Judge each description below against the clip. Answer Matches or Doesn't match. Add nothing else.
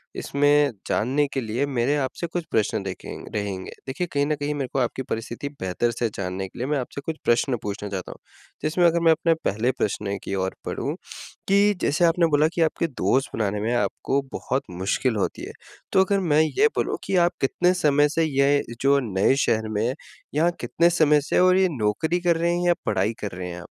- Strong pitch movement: Matches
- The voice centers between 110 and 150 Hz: Matches